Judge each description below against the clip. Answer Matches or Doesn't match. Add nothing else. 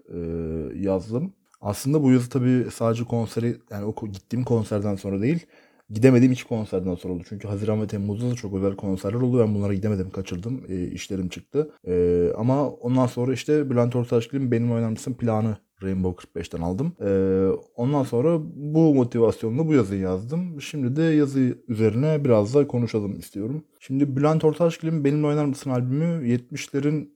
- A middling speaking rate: Doesn't match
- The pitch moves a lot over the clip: Matches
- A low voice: Matches